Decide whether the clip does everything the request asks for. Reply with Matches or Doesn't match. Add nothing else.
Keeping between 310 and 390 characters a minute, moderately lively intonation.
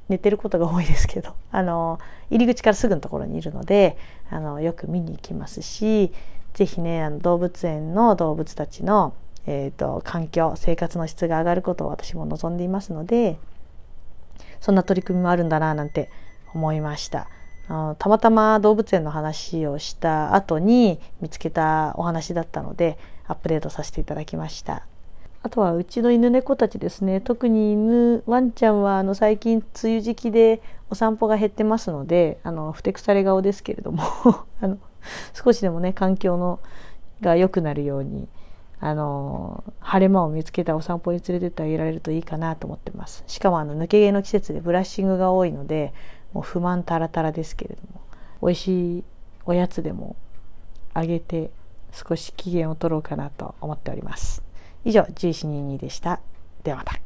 Matches